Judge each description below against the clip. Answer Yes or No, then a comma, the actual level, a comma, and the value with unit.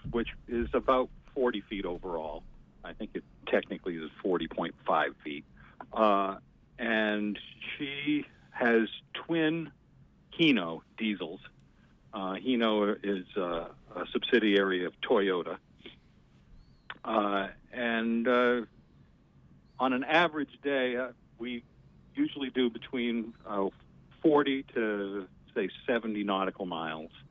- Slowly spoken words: Yes, slow, 105 wpm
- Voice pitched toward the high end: No, low, 115 Hz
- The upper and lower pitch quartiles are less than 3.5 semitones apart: No, average, 4.4 semitones